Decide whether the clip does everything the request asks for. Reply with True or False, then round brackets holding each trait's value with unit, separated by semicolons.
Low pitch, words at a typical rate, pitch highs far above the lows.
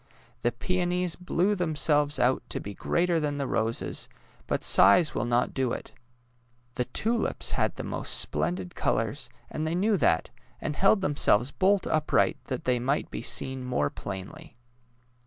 False (145 Hz; 155 wpm; 6.7 semitones)